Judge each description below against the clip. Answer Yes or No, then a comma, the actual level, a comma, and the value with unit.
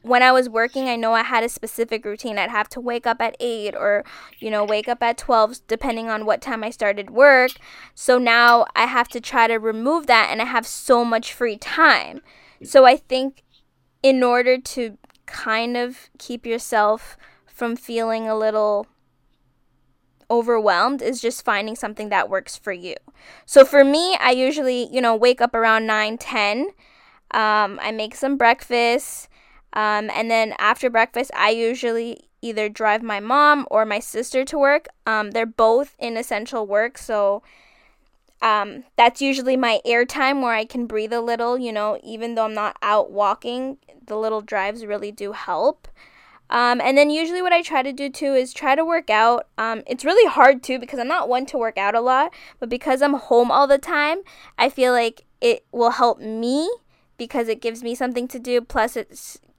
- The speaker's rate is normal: Yes, average, 190 wpm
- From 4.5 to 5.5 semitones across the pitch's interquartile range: No, average, 2.8 semitones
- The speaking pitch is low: No, high, 235 Hz